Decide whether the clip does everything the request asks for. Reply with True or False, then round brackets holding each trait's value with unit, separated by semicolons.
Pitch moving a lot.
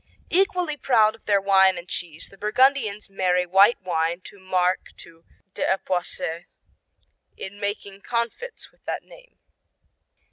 False (4.1 semitones)